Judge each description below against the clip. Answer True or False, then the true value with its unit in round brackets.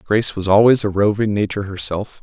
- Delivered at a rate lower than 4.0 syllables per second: False (5.9 syllables/s)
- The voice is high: False (100 Hz)